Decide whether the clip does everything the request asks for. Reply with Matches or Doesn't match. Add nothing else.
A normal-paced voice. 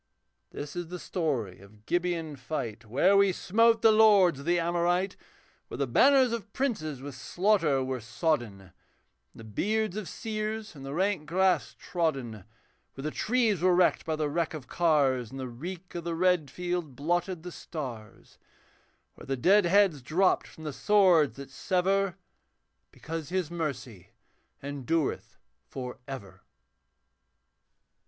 Matches